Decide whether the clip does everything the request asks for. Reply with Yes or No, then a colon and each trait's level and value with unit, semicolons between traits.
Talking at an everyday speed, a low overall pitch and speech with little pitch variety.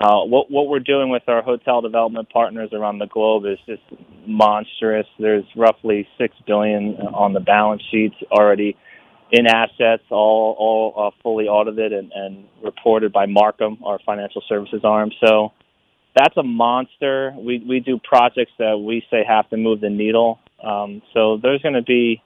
Yes: average, 170 wpm; low, 110 Hz; narrow, 1.8 semitones